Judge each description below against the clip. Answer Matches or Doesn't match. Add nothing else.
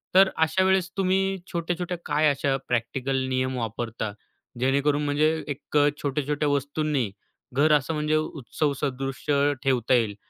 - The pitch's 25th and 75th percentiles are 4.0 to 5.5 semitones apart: Doesn't match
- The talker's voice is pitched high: Doesn't match